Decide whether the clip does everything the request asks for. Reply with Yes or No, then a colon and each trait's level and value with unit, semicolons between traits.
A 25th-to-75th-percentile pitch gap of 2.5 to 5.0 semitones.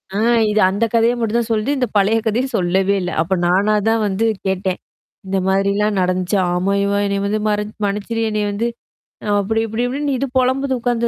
Yes: average, 2.9 semitones